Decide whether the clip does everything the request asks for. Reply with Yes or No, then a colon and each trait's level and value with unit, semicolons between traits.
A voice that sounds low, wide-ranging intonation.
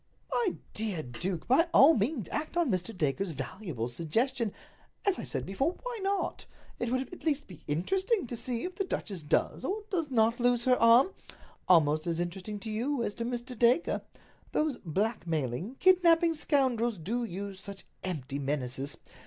No: high, 230 Hz; wide, 8.6 semitones